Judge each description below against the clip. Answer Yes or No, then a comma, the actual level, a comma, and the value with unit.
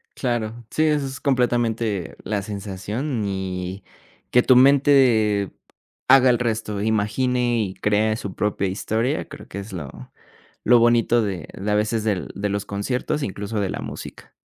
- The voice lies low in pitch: Yes, low, 110 Hz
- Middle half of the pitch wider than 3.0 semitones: Yes, average, 3.6 semitones